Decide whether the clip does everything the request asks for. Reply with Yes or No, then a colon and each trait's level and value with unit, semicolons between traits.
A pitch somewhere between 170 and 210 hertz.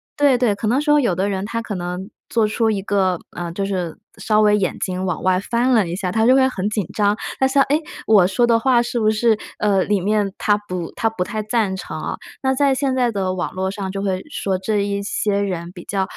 Yes: high, 205 Hz